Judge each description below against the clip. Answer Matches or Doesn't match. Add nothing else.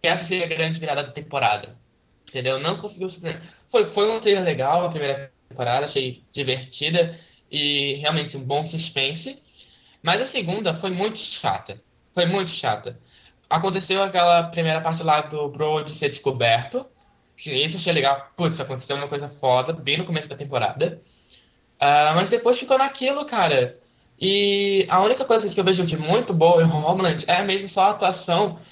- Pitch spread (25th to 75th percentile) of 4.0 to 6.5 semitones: Matches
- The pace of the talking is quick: Doesn't match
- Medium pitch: Matches